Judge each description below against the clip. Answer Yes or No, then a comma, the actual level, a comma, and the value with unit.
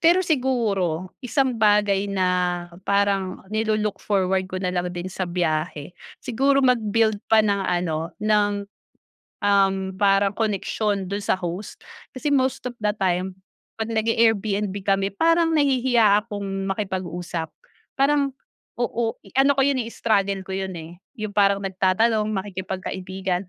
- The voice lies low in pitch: No, high, 200 Hz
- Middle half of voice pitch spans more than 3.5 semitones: No, average, 3.2 semitones